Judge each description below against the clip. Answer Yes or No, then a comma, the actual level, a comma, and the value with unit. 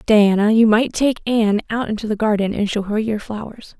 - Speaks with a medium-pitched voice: No, high, 215 Hz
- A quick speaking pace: Yes, fast, 220 wpm